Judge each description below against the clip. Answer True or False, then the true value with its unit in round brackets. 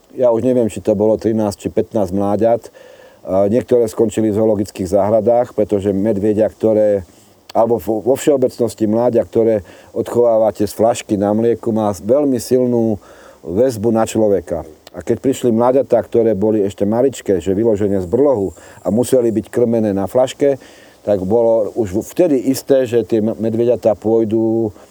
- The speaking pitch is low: True (110 Hz)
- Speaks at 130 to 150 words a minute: True (145 wpm)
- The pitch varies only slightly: True (2.1 semitones)